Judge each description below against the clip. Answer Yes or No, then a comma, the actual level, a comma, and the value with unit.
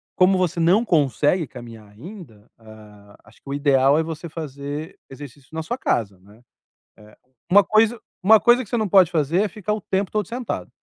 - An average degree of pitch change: No, wide, 7.2 semitones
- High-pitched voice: No, medium, 160 Hz